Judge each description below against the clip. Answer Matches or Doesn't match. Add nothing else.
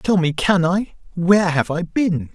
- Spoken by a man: Matches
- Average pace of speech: Matches